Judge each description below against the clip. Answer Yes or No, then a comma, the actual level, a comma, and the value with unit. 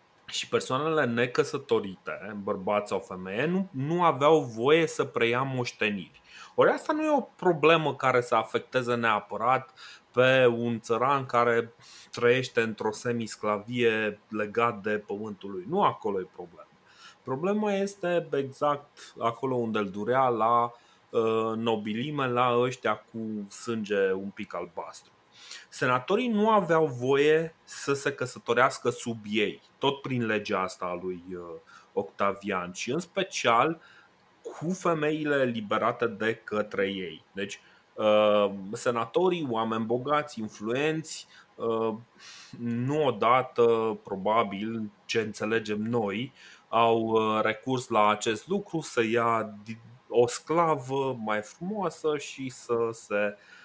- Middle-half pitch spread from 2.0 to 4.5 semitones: No, average, 5.0 semitones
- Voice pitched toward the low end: Yes, low, 120 Hz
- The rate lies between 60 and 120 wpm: Yes, slow, 115 wpm